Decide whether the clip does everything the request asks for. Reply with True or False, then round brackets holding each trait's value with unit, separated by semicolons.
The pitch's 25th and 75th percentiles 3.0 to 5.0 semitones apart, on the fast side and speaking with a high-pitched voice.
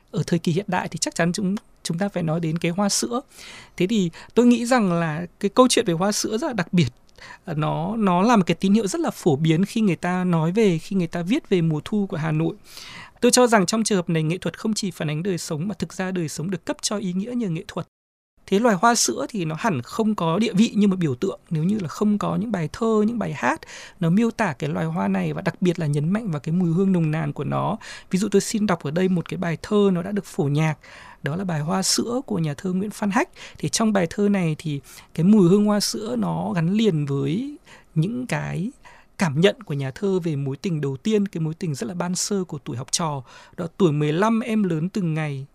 False (4.4 semitones; 270 wpm; 180 Hz)